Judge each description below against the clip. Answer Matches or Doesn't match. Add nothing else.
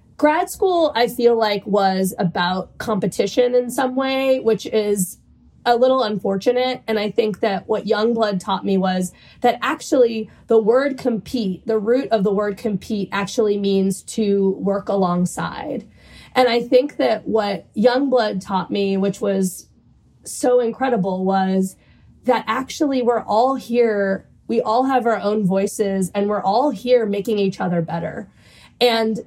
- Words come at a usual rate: Matches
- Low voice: Doesn't match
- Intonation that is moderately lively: Matches